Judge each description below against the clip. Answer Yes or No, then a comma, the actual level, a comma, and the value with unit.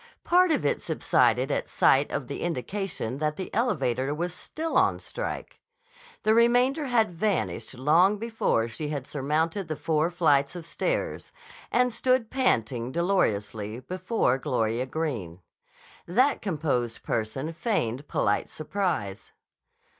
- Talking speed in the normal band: No, slow, 130 wpm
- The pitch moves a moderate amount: No, wide, 8.4 semitones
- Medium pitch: Yes, medium, 160 Hz